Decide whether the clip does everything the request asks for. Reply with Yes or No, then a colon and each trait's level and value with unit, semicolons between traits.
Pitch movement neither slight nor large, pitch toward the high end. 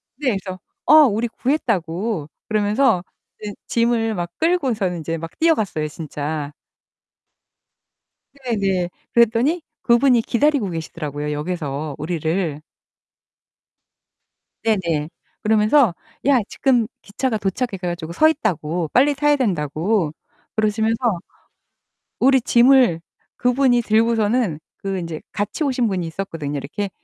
No: wide, 6.5 semitones; high, 205 Hz